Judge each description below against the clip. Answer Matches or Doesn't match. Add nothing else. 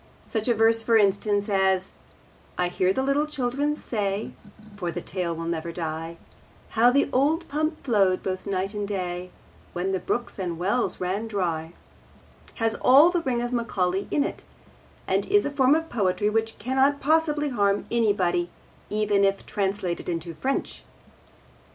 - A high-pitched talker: Matches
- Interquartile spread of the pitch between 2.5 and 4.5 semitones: Doesn't match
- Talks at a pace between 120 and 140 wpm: Doesn't match